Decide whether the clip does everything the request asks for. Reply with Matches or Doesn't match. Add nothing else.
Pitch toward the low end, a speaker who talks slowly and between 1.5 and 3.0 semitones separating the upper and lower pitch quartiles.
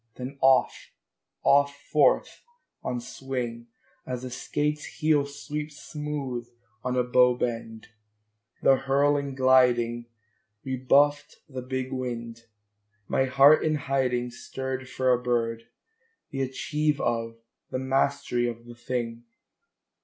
Matches